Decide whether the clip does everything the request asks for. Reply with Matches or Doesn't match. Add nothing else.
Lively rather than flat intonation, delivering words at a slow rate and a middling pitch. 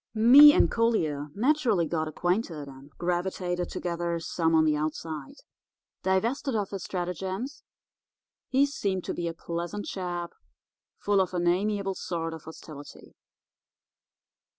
Doesn't match